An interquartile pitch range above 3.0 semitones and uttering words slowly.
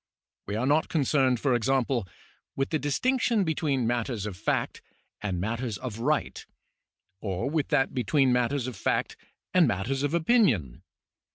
No: average, 4.4 semitones; average, 150 wpm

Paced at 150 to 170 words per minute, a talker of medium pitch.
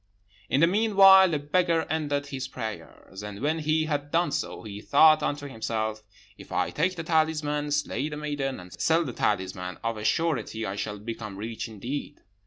No: average, 185 wpm; medium, 145 Hz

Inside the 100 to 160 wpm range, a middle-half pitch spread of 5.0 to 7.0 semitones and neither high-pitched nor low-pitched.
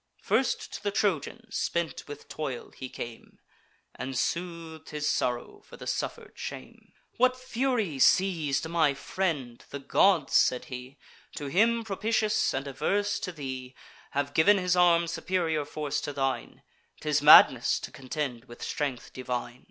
Yes: average, 145 wpm; wide, 5.6 semitones; medium, 150 Hz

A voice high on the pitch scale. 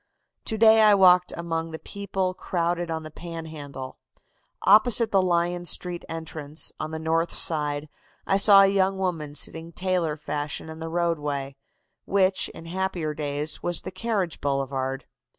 No: medium, 170 Hz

